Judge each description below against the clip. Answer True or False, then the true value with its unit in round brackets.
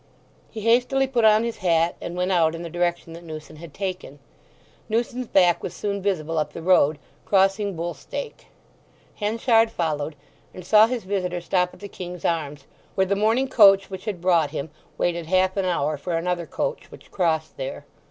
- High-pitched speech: False (180 Hz)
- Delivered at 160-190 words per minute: True (185 wpm)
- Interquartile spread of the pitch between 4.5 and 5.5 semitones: False (3.8 semitones)